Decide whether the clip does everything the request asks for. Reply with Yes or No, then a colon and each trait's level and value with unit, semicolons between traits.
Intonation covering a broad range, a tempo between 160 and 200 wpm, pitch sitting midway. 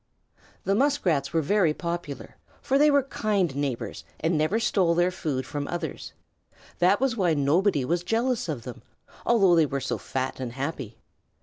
Yes: wide, 6.3 semitones; average, 170 wpm; medium, 170 Hz